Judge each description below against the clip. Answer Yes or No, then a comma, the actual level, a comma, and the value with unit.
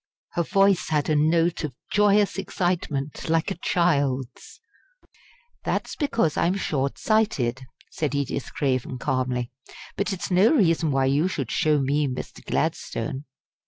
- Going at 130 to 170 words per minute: Yes, slow, 135 wpm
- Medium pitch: Yes, medium, 150 Hz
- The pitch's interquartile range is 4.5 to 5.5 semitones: Yes, average, 5.1 semitones